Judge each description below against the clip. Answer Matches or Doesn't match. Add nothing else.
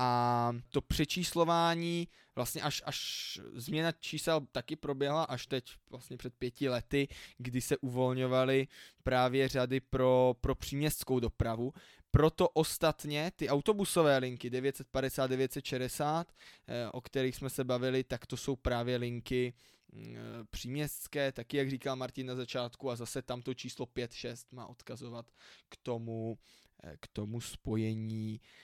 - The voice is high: Doesn't match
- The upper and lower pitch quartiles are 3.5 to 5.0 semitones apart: Doesn't match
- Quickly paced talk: Doesn't match